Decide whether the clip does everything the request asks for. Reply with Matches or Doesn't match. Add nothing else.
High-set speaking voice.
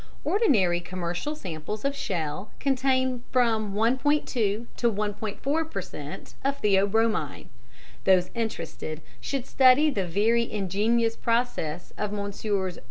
Matches